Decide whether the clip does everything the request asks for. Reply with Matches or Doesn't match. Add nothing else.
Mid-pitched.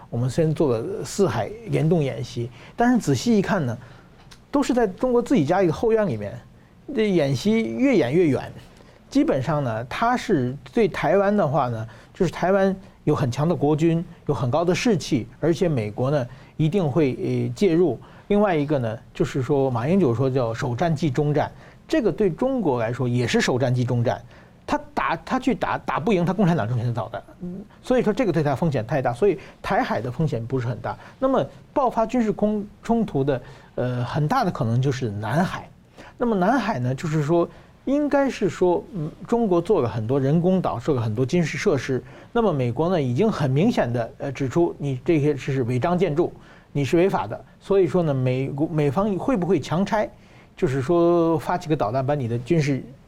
Matches